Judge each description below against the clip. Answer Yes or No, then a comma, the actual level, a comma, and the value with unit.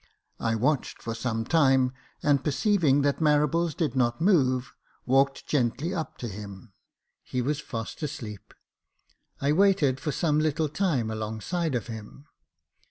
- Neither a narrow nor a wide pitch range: Yes, average, 4.6 semitones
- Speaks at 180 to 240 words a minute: No, average, 140 wpm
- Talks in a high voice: No, low, 135 Hz